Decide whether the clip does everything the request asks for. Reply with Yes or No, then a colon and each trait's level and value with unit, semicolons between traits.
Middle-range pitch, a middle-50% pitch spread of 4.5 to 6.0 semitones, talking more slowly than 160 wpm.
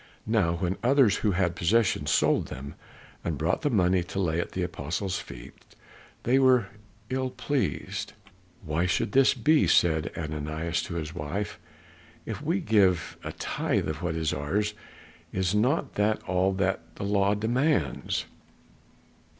No: very low, 95 Hz; average, 4.8 semitones; average, 150 wpm